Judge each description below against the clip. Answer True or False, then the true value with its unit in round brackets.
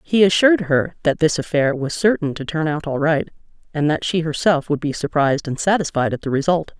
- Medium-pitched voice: True (160 Hz)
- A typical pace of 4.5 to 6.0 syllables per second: True (5.7 syllables/s)